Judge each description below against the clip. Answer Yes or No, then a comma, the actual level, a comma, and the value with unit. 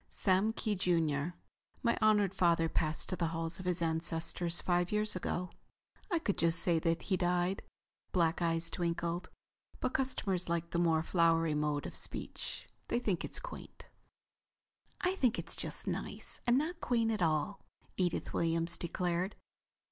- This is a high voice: No, medium, 175 Hz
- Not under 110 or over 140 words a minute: No, average, 155 wpm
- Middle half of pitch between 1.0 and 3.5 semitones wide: Yes, average, 3.1 semitones